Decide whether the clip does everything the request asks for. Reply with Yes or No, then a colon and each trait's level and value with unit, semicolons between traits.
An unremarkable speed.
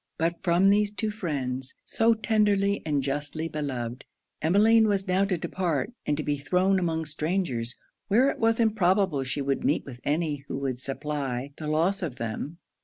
Yes: average, 175 wpm